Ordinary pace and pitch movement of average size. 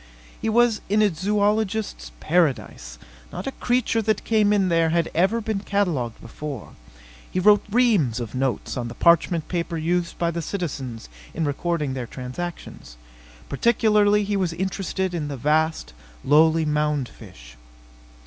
No: average, 150 wpm; wide, 6.2 semitones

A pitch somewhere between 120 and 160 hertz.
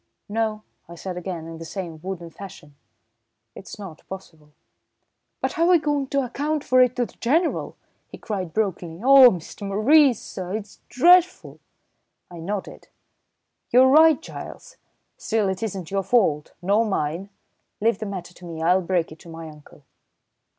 No: high, 200 Hz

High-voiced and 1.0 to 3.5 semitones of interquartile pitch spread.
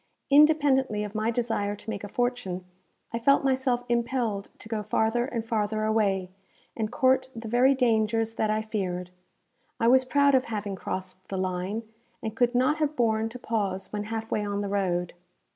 Yes: high, 225 Hz; average, 3.2 semitones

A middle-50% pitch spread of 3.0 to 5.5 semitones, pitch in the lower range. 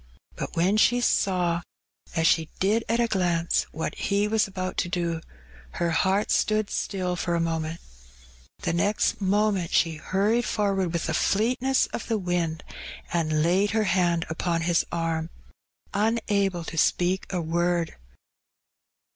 No: average, 3.5 semitones; medium, 180 Hz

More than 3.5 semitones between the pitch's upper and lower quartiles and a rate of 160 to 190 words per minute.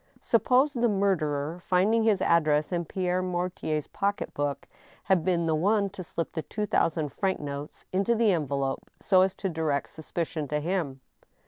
Yes: average, 4.3 semitones; average, 165 wpm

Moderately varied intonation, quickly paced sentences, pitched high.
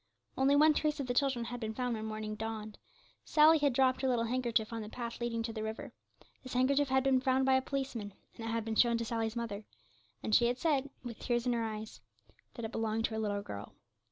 Yes: average, 3.0 semitones; fast, 240 wpm; high, 235 Hz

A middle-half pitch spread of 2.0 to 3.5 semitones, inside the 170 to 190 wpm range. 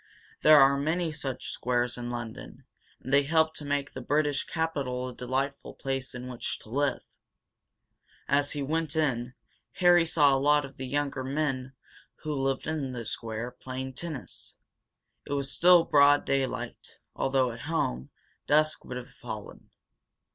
No: average, 2.7 semitones; average, 155 wpm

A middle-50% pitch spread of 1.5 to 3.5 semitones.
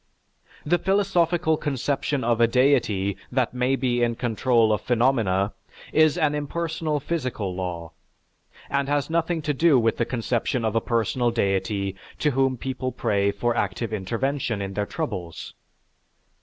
No: average, 5.1 semitones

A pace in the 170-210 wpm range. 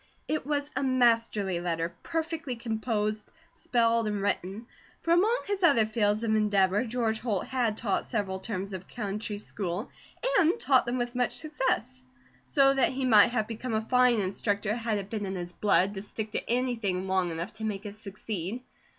Yes: average, 180 wpm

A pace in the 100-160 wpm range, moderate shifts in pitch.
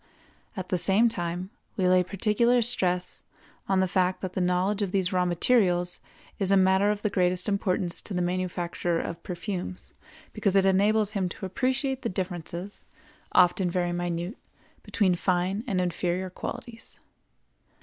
No: average, 155 wpm; narrow, 2.2 semitones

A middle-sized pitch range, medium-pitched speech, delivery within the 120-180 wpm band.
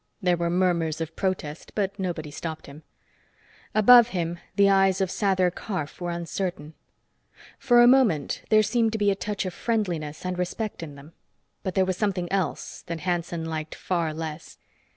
Yes: average, 3.4 semitones; medium, 180 Hz; average, 170 wpm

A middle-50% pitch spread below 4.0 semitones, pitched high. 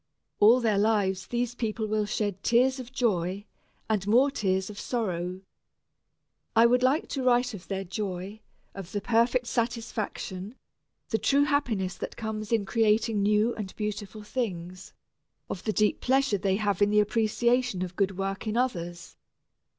Yes: average, 3.6 semitones; high, 215 Hz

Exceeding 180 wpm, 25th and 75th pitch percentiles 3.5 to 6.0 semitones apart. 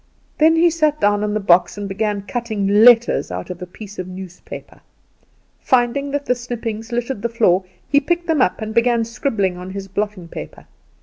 Yes: average, 190 wpm; average, 4.0 semitones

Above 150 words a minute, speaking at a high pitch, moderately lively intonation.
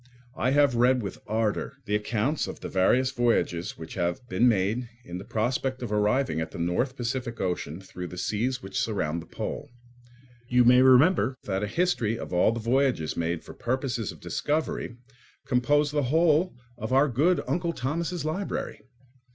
No: average, 175 wpm; low, 120 Hz; average, 4.9 semitones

